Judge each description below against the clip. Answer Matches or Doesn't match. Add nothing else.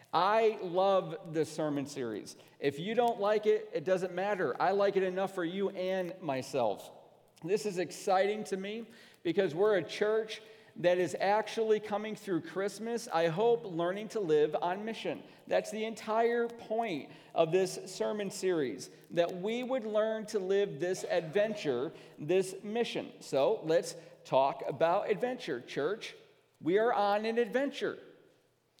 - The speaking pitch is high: Matches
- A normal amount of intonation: Matches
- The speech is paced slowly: Doesn't match